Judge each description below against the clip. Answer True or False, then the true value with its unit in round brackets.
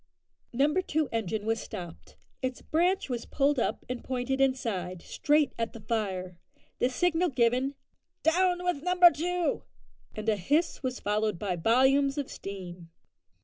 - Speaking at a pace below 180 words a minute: True (145 wpm)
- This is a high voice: True (255 Hz)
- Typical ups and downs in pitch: False (6.0 semitones)